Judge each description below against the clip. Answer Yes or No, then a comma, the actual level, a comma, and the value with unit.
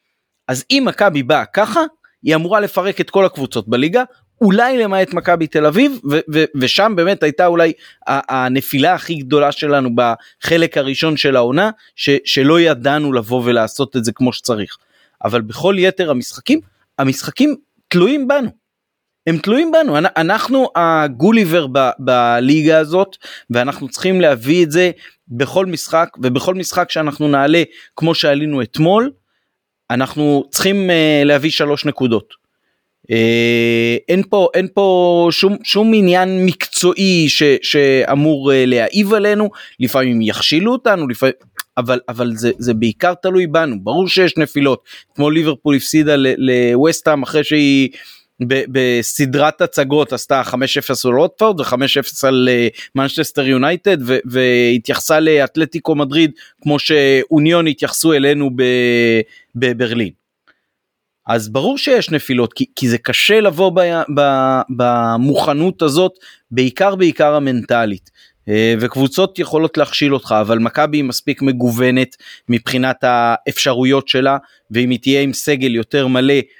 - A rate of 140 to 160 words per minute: No, average, 130 wpm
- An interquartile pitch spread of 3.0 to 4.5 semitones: No, average, 5.3 semitones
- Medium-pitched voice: Yes, medium, 145 Hz